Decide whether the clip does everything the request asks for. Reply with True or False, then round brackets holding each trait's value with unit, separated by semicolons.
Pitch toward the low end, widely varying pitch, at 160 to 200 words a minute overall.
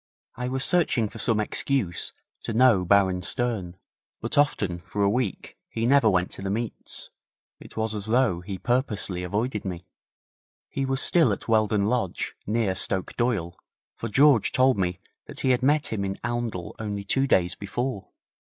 False (110 Hz; 4.6 semitones; 170 wpm)